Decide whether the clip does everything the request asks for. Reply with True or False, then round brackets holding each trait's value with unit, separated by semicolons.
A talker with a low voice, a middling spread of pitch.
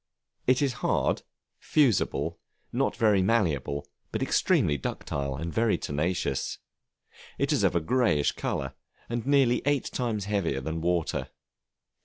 False (95 Hz; 7.8 semitones)